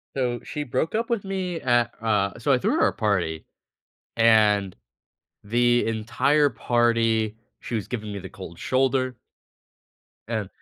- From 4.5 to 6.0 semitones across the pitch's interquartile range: No, average, 3.4 semitones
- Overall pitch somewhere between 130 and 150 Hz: No, low, 115 Hz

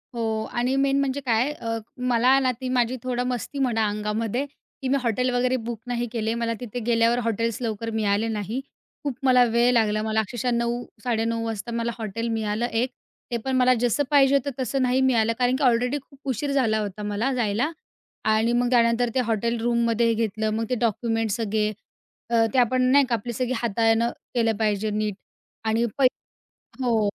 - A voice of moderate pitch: No, high, 235 Hz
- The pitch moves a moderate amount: No, narrow, 2.2 semitones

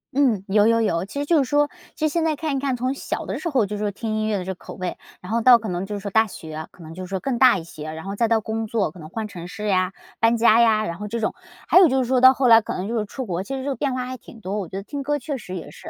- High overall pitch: Yes, high, 220 Hz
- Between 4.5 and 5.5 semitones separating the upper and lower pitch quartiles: Yes, average, 5.2 semitones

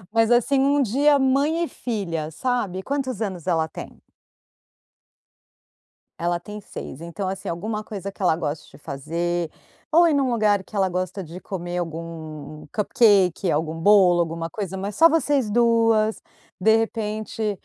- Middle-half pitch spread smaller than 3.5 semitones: No, average, 5.0 semitones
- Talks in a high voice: Yes, high, 200 Hz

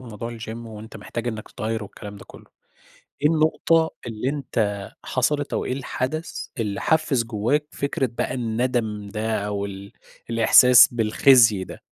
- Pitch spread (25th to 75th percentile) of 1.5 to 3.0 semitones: No, average, 3.6 semitones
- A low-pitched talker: Yes, low, 115 Hz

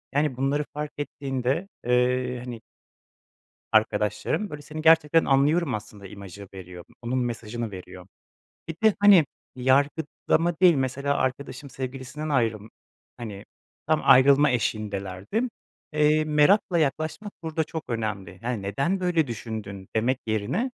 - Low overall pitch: Yes, low, 130 Hz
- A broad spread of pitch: Yes, wide, 5.9 semitones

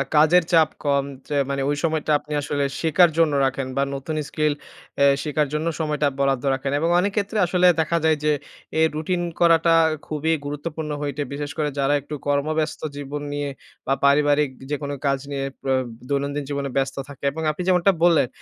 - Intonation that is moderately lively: No, narrow, 2.2 semitones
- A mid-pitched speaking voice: Yes, medium, 150 Hz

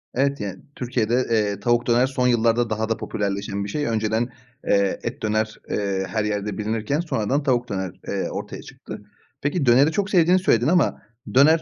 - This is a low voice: Yes, low, 115 Hz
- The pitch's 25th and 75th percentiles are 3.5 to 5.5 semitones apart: Yes, average, 4.4 semitones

